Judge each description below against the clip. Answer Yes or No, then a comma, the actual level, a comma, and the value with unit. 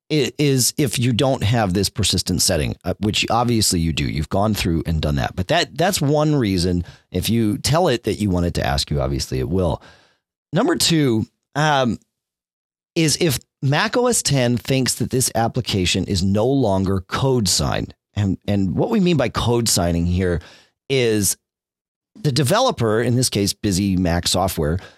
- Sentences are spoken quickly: No, average, 175 wpm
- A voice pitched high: No, low, 100 Hz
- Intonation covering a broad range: Yes, wide, 6.3 semitones